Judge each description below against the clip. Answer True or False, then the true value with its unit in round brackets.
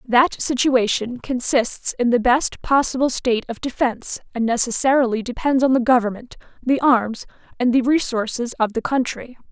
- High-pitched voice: True (245 Hz)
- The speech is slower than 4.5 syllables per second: False (5.0 syllables/s)